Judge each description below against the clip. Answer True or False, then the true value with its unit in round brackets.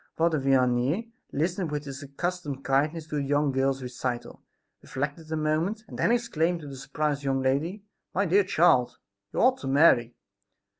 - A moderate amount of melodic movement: True (4.0 semitones)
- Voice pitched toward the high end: False (150 Hz)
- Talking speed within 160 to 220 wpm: True (165 wpm)